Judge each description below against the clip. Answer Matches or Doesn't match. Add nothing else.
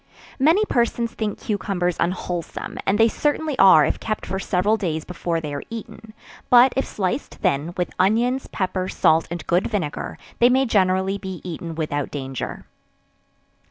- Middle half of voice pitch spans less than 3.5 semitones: Doesn't match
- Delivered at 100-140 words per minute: Doesn't match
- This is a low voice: Doesn't match